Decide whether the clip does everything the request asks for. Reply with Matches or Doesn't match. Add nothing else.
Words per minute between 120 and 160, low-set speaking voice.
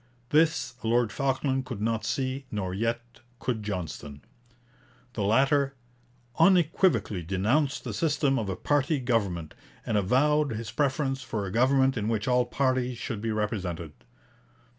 Matches